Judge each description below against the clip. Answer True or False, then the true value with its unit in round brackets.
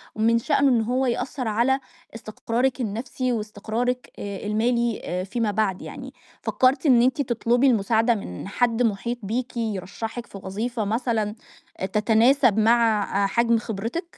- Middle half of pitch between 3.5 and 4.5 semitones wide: False (2.7 semitones)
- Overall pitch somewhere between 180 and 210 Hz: False (230 Hz)